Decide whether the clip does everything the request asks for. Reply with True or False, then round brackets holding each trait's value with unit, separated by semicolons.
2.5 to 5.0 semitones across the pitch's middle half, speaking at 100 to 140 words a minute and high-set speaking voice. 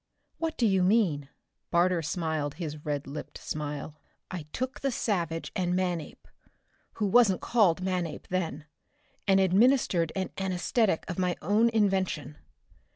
False (4.0 semitones; 135 wpm; 180 Hz)